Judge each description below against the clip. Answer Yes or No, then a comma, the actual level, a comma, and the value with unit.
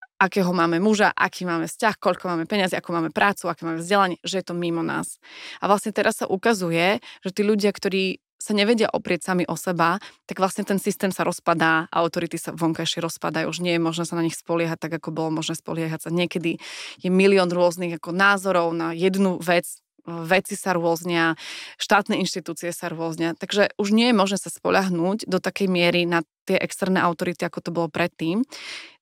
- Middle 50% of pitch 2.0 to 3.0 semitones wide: Yes, narrow, 2.6 semitones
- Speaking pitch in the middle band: Yes, medium, 175 Hz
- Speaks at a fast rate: Yes, fast, 190 wpm